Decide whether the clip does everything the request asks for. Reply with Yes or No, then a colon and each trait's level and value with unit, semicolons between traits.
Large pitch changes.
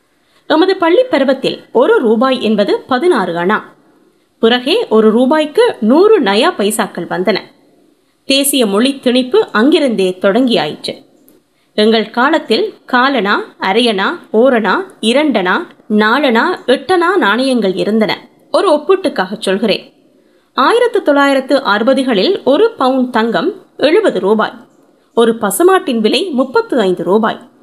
Yes: wide, 7.1 semitones